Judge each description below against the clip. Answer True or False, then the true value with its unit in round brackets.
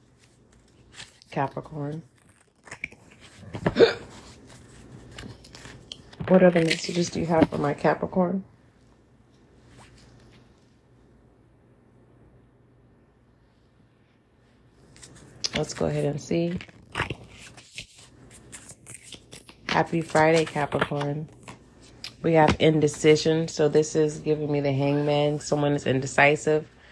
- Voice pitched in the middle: True (145 Hz)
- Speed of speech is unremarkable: False (70 wpm)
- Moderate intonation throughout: True (3.6 semitones)